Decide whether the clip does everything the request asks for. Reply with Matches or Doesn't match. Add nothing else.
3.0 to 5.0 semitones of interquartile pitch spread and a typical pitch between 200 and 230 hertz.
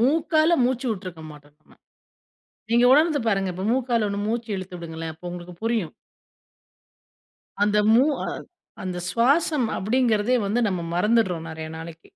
Doesn't match